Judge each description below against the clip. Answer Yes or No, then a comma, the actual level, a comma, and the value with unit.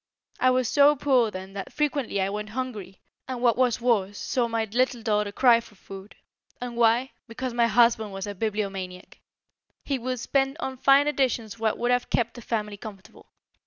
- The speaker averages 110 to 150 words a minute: No, average, 185 wpm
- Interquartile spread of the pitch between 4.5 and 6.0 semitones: No, average, 3.5 semitones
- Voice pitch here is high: Yes, high, 230 Hz